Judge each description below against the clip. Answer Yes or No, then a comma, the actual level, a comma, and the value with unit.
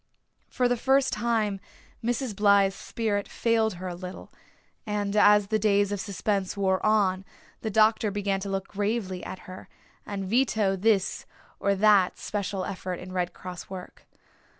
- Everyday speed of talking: Yes, average, 155 wpm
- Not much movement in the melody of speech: Yes, narrow, 2.2 semitones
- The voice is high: Yes, high, 200 Hz